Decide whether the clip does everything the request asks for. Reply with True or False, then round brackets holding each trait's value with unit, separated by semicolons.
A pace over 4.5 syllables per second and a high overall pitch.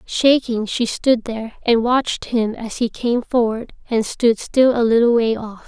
False (4.3 syllables/s; 230 Hz)